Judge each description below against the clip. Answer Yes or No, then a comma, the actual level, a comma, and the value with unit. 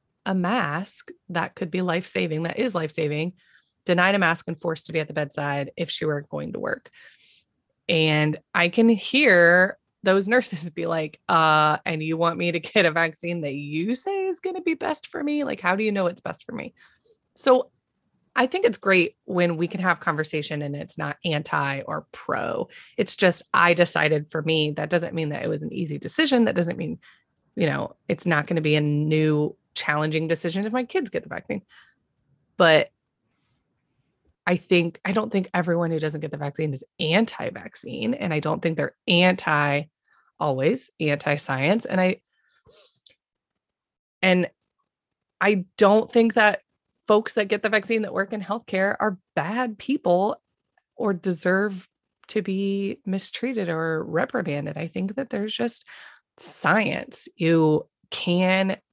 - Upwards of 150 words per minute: Yes, average, 170 wpm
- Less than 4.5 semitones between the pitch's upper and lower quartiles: No, average, 4.8 semitones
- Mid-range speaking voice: Yes, medium, 175 Hz